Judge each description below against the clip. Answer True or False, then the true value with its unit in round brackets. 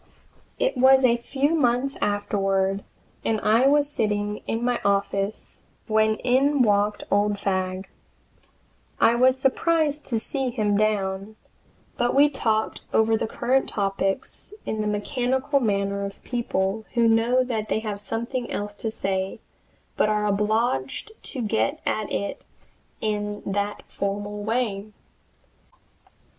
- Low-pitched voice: False (215 Hz)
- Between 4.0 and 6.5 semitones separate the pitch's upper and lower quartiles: False (3.6 semitones)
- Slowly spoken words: True (130 wpm)